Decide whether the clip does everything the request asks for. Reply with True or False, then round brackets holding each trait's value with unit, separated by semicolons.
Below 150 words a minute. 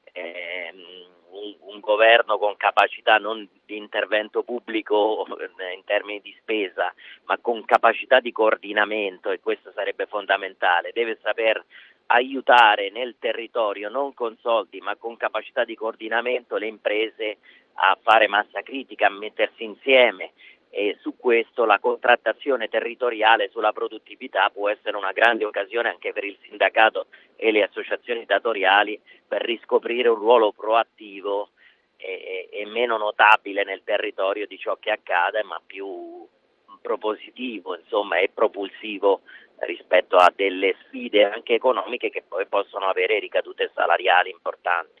True (130 wpm)